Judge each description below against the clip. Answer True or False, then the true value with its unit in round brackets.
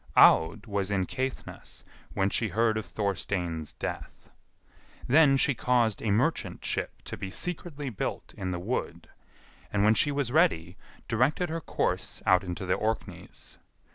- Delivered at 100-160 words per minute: True (150 wpm)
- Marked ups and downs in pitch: True (5.9 semitones)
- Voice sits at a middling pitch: False (110 Hz)